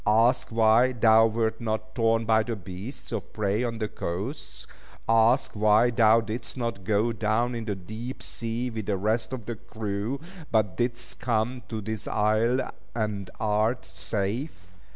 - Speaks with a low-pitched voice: Yes, low, 110 Hz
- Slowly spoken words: No, average, 160 wpm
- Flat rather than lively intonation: Yes, narrow, 1.8 semitones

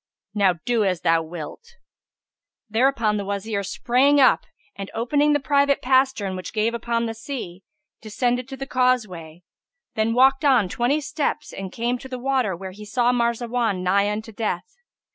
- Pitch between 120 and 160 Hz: No, high, 235 Hz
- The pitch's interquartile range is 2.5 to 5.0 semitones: Yes, average, 4.5 semitones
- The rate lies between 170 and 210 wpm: No, average, 160 wpm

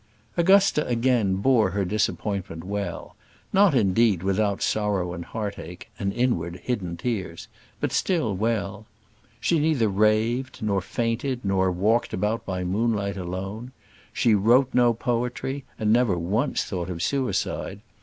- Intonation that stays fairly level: No, average, 4.2 semitones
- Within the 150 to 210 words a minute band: No, slow, 135 wpm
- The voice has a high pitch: No, low, 105 Hz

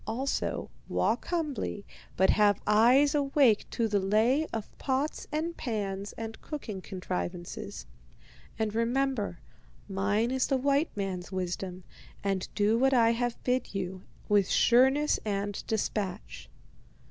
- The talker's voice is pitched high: Yes, high, 220 Hz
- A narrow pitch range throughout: No, average, 5.0 semitones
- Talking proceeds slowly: Yes, slow, 125 wpm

